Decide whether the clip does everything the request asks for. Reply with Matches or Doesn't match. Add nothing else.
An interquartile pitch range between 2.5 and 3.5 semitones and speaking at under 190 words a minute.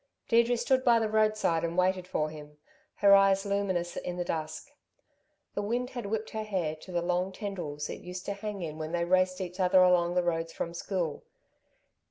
Doesn't match